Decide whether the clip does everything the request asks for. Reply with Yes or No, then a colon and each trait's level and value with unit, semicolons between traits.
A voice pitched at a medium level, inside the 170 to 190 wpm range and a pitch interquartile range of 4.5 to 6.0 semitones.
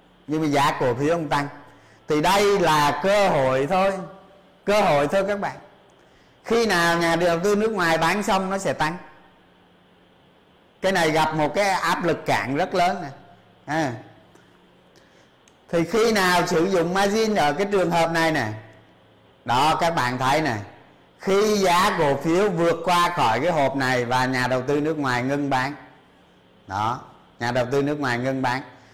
Yes: medium, 155 Hz; average, 175 wpm; wide, 5.5 semitones